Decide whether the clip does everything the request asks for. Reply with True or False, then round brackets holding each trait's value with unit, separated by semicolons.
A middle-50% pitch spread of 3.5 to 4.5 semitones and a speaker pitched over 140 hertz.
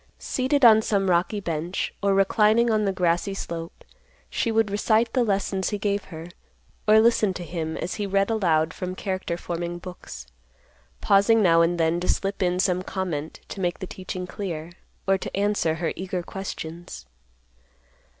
False (3.1 semitones; 190 Hz)